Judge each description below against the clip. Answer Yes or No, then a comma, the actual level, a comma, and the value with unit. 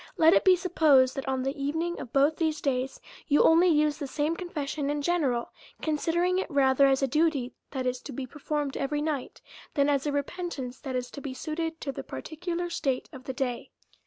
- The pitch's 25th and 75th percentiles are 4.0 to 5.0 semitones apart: No, average, 3.4 semitones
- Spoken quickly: Yes, fast, 215 wpm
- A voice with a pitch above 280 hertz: Yes, very high, 290 Hz